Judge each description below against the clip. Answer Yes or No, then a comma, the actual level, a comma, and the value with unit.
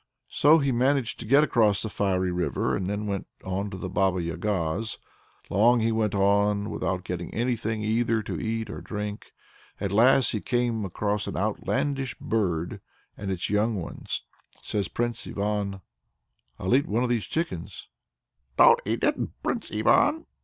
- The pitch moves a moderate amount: Yes, average, 3.4 semitones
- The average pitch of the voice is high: No, low, 105 Hz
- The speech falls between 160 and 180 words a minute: Yes, average, 165 wpm